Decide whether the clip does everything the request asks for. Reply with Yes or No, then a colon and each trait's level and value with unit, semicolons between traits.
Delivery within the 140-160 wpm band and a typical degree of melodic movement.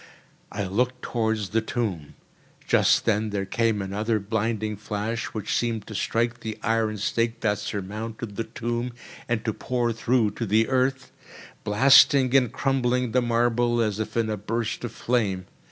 No: average, 155 wpm; narrow, 2.2 semitones